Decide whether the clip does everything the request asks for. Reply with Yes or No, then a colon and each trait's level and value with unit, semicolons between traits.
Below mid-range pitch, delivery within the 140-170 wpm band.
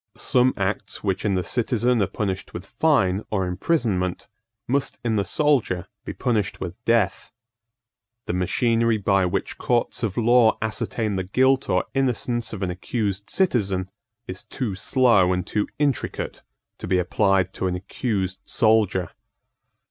Yes: low, 105 Hz; average, 150 wpm